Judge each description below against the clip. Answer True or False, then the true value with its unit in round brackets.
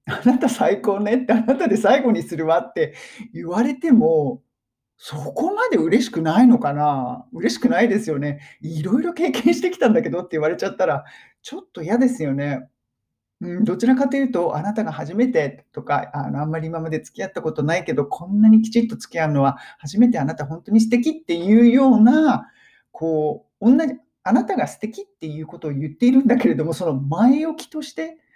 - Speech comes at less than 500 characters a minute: True (395 characters per minute)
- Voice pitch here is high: True (210 Hz)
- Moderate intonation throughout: False (8.0 semitones)